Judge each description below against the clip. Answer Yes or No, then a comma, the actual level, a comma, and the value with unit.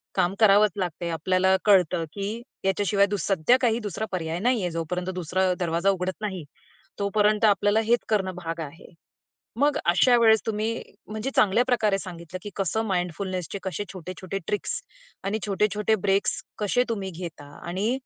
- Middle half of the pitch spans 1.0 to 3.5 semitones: Yes, average, 2.9 semitones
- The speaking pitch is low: No, high, 195 Hz